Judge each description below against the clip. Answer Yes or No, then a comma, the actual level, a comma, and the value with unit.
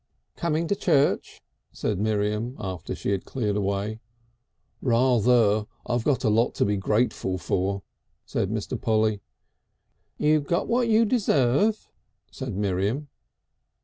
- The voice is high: No, low, 115 Hz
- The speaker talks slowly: Yes, slow, 125 wpm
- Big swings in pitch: Yes, wide, 5.8 semitones